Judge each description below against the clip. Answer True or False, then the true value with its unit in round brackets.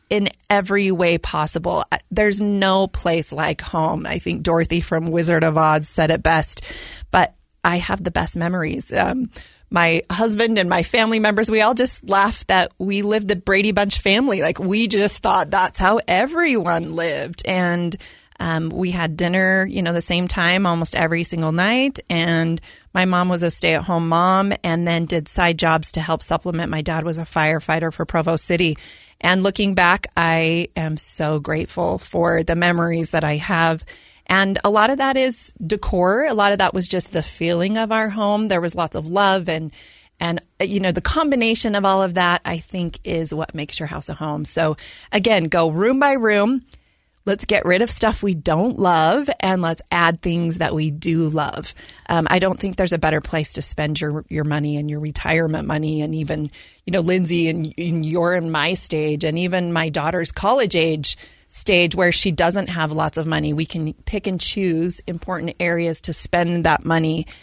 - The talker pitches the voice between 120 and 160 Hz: False (170 Hz)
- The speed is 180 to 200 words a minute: True (195 wpm)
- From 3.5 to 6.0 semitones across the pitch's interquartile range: False (3.0 semitones)